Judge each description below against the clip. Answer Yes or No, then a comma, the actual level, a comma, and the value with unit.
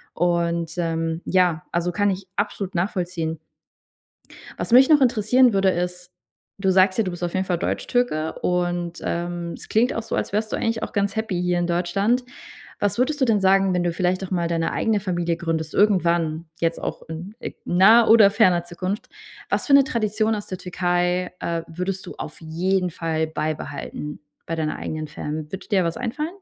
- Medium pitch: Yes, medium, 180 Hz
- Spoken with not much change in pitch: No, average, 3.3 semitones